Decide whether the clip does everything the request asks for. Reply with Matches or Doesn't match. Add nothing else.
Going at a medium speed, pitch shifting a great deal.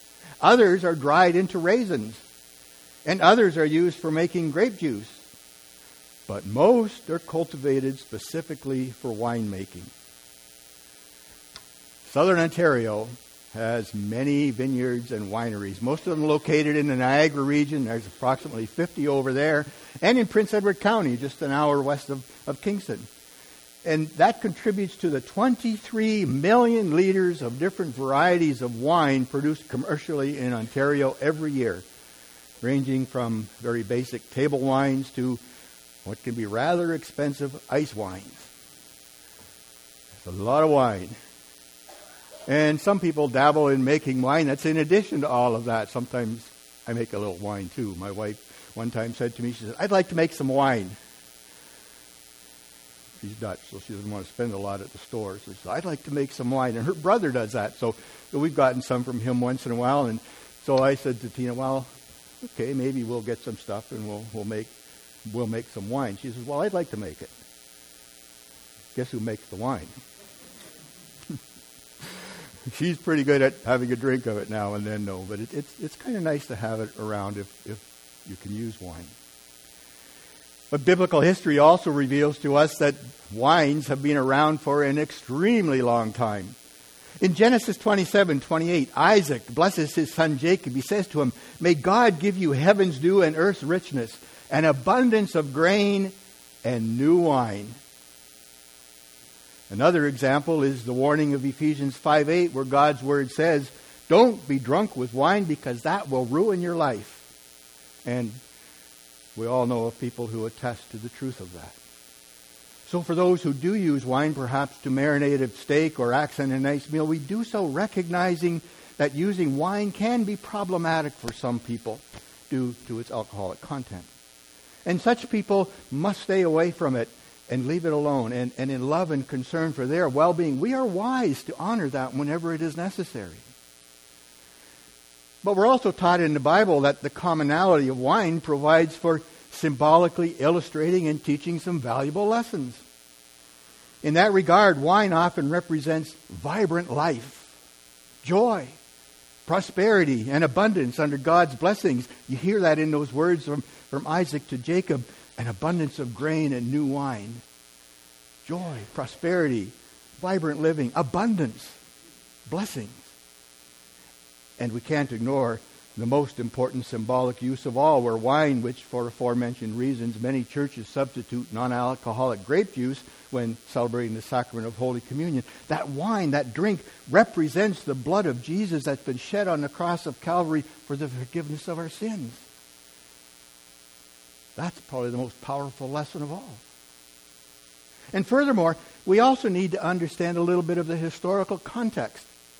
Matches